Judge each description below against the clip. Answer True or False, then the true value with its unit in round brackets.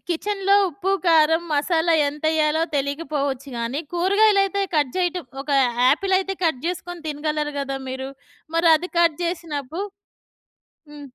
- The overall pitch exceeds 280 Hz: True (320 Hz)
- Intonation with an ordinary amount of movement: True (3.6 semitones)